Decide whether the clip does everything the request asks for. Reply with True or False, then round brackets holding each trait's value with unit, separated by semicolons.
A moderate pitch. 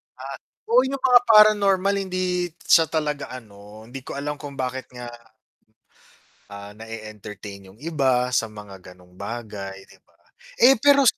False (130 Hz)